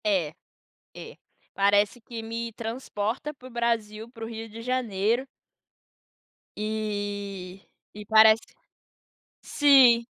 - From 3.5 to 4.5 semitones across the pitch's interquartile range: No, narrow, 2.4 semitones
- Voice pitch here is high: Yes, high, 220 Hz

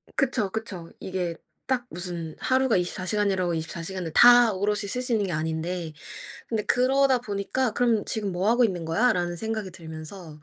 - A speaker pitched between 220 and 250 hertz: No, high, 195 Hz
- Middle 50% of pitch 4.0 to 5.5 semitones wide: Yes, average, 5.1 semitones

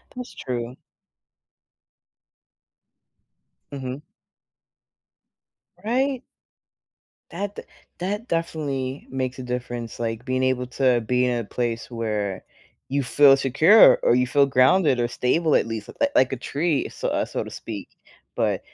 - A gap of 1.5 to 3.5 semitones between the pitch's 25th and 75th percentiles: No, average, 4.2 semitones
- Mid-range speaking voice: No, low, 130 Hz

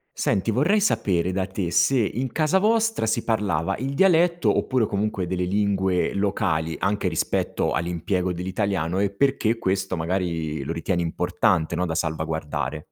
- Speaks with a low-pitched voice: Yes, very low, 95 Hz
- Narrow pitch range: No, average, 4.6 semitones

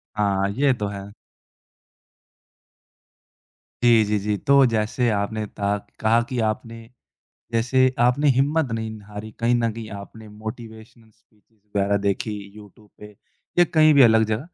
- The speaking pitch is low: Yes, low, 110 Hz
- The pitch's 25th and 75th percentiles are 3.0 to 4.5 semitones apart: No, narrow, 2.4 semitones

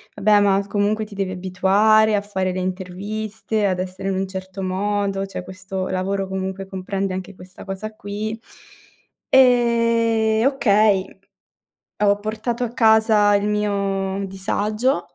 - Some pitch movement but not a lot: No, narrow, 2.2 semitones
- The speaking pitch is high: Yes, high, 200 Hz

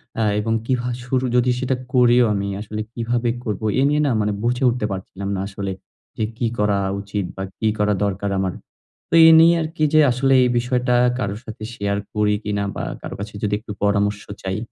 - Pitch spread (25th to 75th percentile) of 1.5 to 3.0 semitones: No, average, 3.4 semitones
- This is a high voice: No, low, 110 Hz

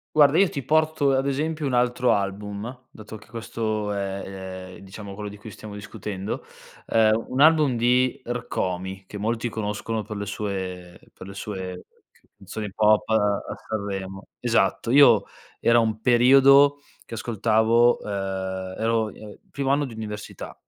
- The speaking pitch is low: Yes, low, 110 Hz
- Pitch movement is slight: No, average, 3.7 semitones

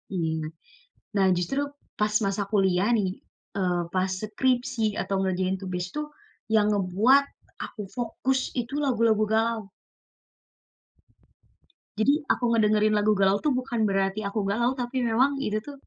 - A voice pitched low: No, high, 215 Hz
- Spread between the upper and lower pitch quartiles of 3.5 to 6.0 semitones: Yes, average, 3.9 semitones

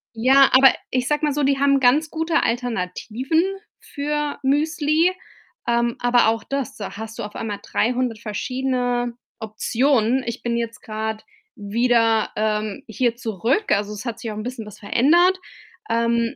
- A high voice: Yes, high, 240 Hz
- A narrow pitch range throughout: No, average, 3.7 semitones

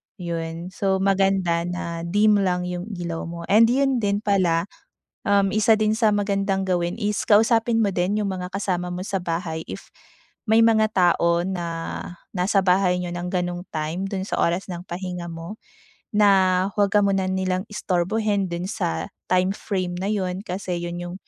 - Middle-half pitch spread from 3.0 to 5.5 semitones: No, narrow, 2.6 semitones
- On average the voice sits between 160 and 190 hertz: Yes, medium, 185 Hz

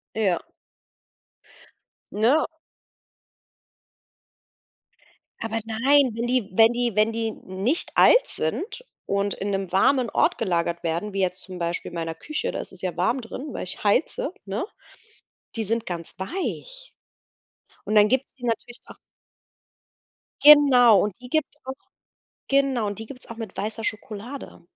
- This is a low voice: No, high, 225 Hz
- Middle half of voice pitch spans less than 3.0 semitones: No, average, 4.8 semitones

